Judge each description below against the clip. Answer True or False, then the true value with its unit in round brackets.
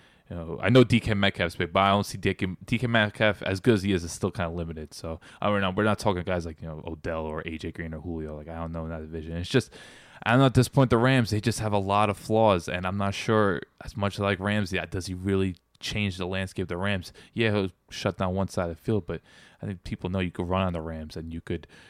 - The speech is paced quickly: True (290 wpm)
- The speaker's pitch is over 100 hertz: False (95 Hz)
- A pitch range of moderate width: True (3.7 semitones)